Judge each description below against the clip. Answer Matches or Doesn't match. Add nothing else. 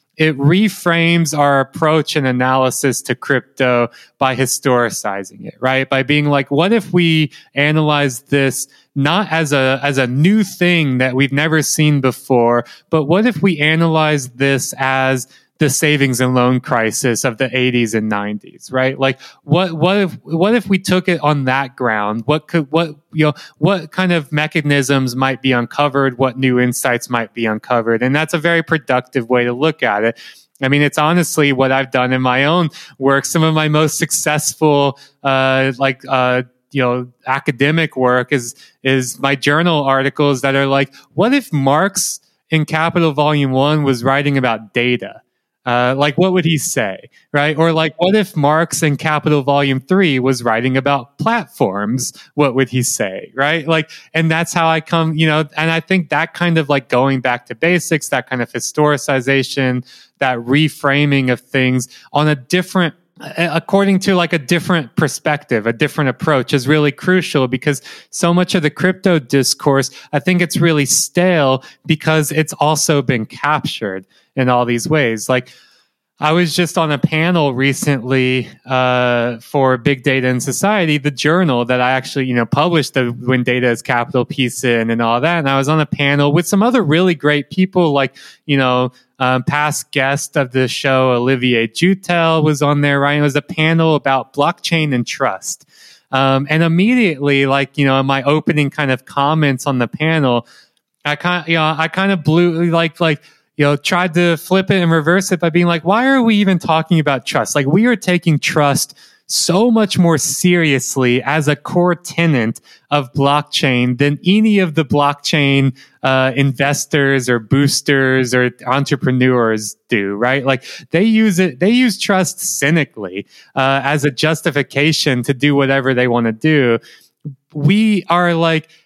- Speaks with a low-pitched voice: Doesn't match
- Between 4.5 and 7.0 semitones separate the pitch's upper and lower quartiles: Doesn't match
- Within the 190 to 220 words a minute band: Doesn't match